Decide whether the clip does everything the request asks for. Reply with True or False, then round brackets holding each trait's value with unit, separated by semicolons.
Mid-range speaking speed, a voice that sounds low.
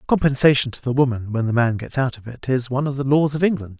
False (285 wpm; 130 Hz)